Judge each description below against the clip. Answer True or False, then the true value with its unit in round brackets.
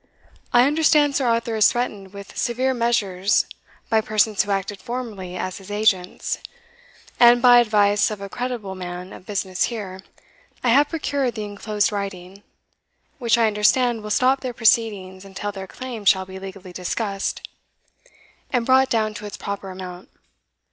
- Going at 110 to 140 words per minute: False (155 wpm)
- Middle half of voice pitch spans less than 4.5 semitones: True (3.8 semitones)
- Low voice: False (210 Hz)